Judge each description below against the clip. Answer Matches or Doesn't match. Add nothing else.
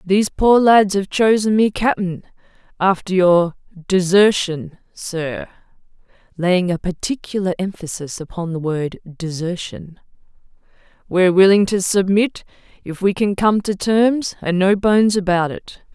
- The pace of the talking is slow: Matches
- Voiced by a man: Doesn't match